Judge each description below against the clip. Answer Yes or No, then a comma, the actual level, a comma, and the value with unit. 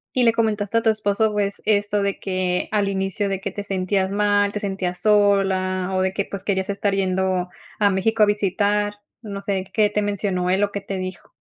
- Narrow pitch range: Yes, narrow, 1.5 semitones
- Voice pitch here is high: Yes, high, 200 Hz